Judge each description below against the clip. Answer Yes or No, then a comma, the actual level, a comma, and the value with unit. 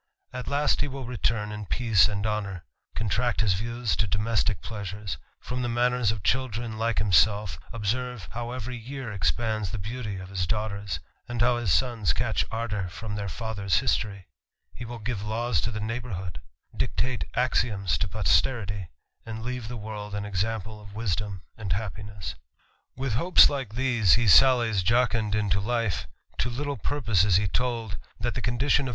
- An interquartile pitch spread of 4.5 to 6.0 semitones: No, average, 3.2 semitones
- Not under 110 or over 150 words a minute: No, average, 170 wpm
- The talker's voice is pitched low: Yes, low, 110 Hz